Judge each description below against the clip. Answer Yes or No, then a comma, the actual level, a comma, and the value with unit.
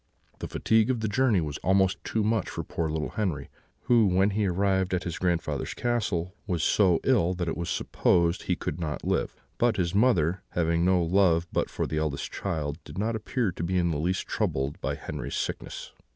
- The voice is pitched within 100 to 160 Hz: No, very low, 90 Hz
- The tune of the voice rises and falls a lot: No, average, 3.8 semitones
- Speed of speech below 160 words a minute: No, fast, 205 wpm